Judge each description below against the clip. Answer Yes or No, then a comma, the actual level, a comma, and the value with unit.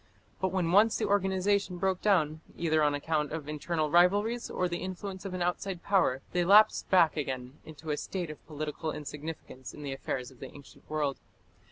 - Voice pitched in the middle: Yes, medium, 165 Hz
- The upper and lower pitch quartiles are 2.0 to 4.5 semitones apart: Yes, average, 4.0 semitones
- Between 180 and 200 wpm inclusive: Yes, average, 190 wpm